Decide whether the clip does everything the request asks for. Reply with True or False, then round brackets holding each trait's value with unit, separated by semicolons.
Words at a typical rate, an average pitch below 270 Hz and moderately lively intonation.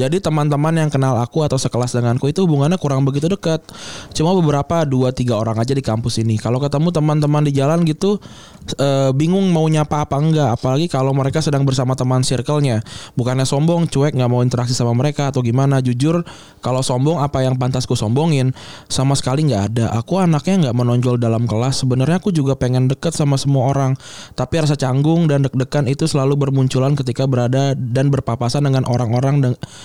False (185 wpm; 135 Hz; 3.0 semitones)